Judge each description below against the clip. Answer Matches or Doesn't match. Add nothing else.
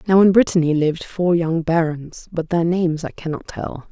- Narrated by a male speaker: Doesn't match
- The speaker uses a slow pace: Doesn't match